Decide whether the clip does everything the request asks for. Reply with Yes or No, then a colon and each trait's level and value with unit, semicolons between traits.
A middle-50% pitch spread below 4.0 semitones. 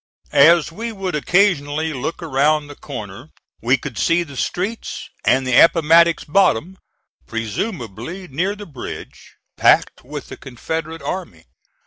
No: average, 5.1 semitones